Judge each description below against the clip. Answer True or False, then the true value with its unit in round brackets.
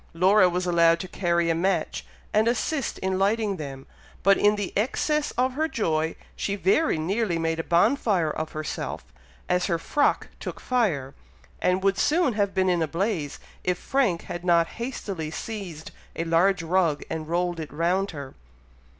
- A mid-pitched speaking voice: True (180 Hz)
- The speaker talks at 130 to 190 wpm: True (170 wpm)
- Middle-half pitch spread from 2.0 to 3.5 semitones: False (3.9 semitones)